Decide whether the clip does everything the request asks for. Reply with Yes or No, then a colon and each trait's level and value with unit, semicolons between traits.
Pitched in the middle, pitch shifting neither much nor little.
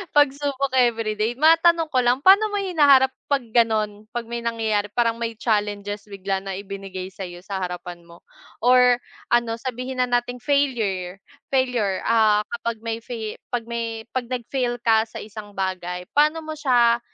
No: high, 230 Hz; average, 3.7 semitones